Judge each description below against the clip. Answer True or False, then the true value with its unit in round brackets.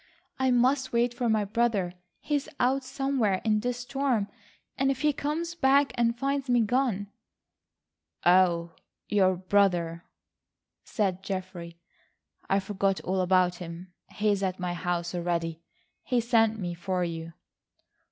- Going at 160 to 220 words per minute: False (135 wpm)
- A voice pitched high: True (205 Hz)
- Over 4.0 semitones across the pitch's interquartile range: True (5.6 semitones)